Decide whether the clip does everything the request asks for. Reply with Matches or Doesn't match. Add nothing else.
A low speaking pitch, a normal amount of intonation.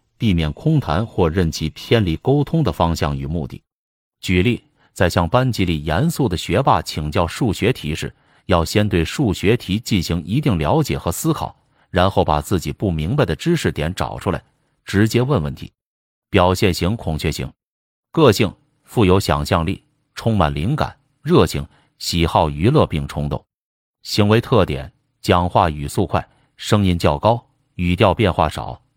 Doesn't match